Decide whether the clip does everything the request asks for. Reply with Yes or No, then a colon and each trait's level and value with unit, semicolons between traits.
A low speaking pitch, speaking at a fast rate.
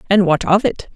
No: high, 190 Hz; fast, 250 wpm